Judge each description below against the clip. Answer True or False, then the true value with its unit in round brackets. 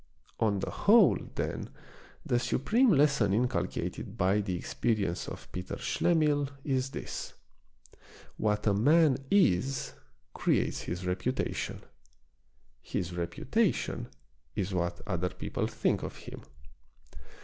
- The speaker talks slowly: True (110 wpm)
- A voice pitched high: False (115 Hz)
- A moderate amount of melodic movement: False (7.8 semitones)